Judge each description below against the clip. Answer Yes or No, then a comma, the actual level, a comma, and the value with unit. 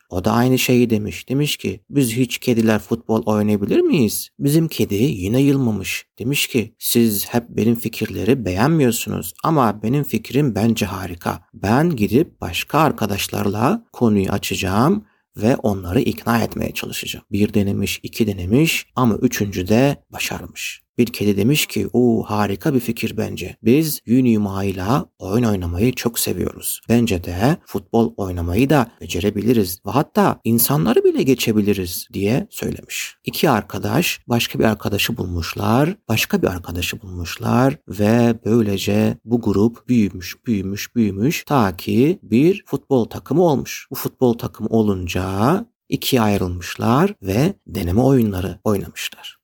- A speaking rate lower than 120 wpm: No, average, 135 wpm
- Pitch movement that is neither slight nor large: Yes, average, 3.9 semitones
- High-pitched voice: No, low, 115 Hz